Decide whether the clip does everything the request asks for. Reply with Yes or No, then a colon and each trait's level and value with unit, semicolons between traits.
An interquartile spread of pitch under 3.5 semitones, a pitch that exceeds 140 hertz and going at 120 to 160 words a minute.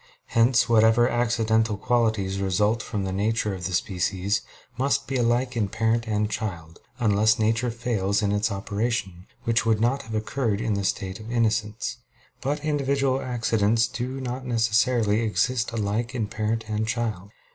No: narrow, 2.6 semitones; low, 110 Hz; average, 155 wpm